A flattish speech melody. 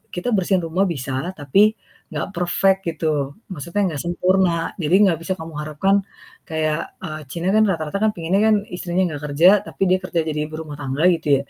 No: average, 3.2 semitones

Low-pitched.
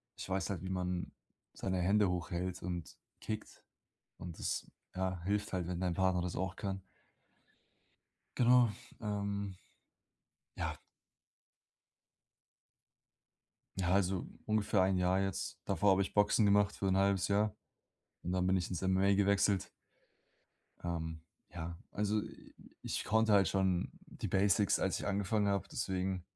Yes: very low, 95 Hz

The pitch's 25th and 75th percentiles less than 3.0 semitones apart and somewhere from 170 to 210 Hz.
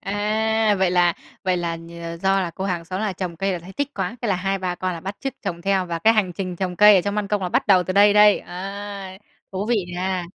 Yes: narrow, 2.4 semitones; high, 190 Hz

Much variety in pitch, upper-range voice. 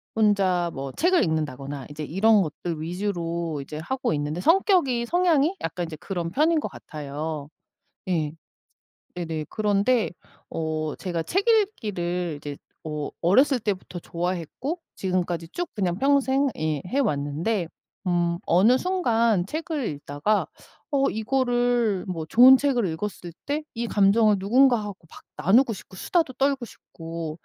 Yes: wide, 7.7 semitones; high, 195 Hz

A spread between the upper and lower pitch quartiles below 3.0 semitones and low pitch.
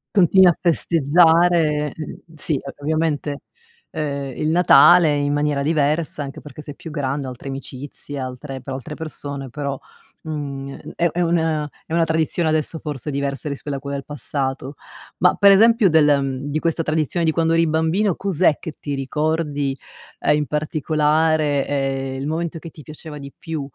No: narrow, 2.5 semitones; medium, 150 Hz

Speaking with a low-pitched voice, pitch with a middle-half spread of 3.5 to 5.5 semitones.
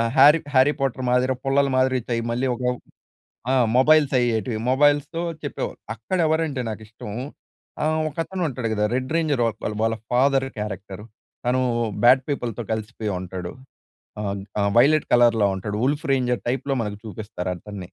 Yes: low, 125 Hz; average, 4.2 semitones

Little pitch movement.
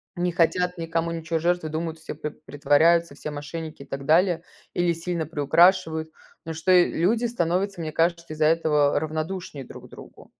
Yes: narrow, 2.1 semitones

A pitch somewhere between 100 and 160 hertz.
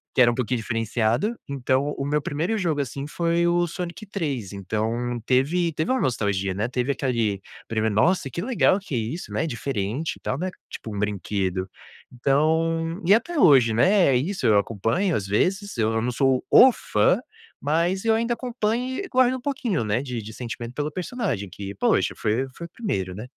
Yes: low, 135 Hz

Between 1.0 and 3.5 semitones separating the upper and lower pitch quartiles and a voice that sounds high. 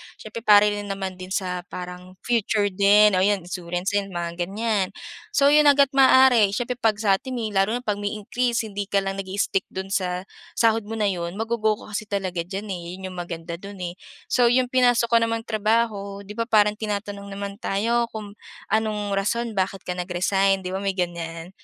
Yes: average, 2.9 semitones; high, 200 Hz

